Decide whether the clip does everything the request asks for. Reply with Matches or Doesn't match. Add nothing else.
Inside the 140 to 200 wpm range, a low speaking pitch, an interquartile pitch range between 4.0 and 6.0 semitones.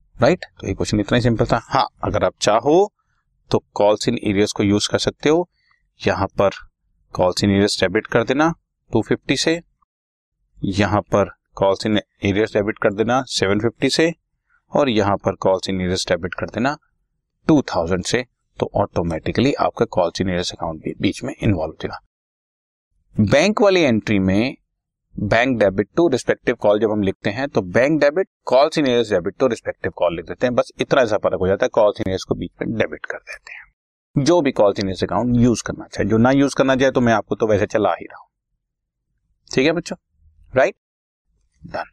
Matches